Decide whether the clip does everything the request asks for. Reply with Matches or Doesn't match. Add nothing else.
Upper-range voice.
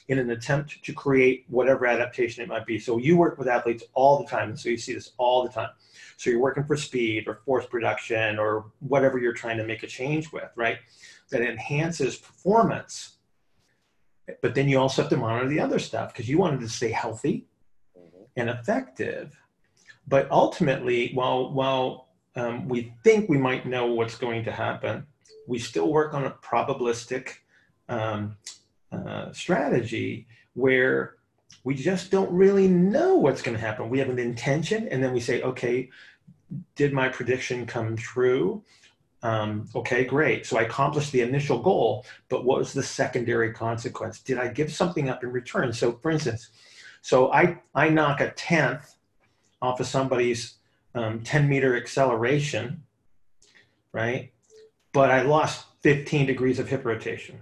Doesn't match